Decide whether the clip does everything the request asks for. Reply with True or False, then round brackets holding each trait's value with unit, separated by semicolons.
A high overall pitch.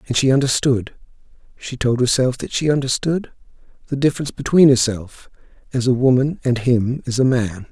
False (130 Hz)